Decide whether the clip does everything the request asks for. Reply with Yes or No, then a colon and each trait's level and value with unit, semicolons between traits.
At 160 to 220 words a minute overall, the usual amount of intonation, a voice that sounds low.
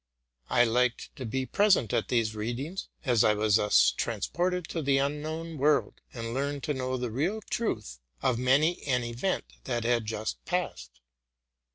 Yes: average, 170 wpm; average, 4.9 semitones; low, 130 Hz